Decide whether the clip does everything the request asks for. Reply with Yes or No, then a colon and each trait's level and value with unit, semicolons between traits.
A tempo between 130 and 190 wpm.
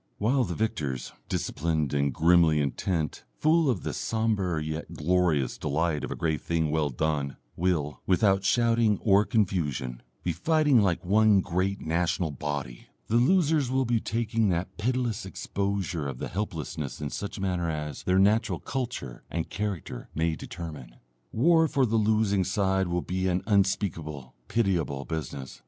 Yes: average, 150 wpm